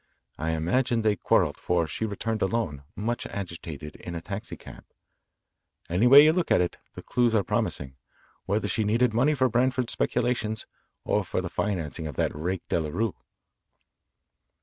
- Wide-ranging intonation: Yes, wide, 6.1 semitones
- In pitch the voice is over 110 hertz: No, low, 105 Hz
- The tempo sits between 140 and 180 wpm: Yes, average, 160 wpm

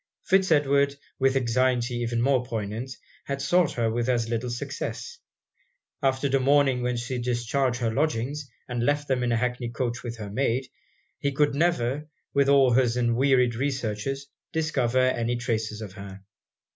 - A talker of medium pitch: No, low, 125 Hz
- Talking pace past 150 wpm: Yes, average, 160 wpm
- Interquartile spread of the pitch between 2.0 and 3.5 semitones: Yes, average, 2.8 semitones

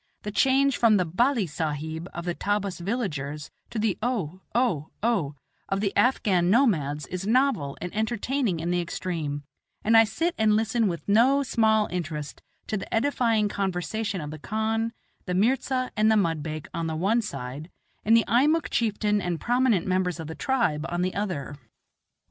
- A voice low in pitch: No, high, 200 Hz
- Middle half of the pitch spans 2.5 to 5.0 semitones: No, wide, 5.4 semitones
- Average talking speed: Yes, average, 170 wpm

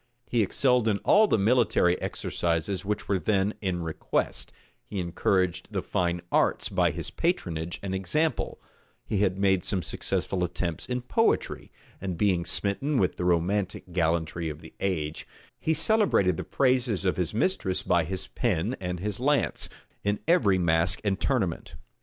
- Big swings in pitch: No, average, 4.1 semitones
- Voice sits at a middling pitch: No, very low, 95 Hz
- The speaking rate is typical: Yes, average, 160 wpm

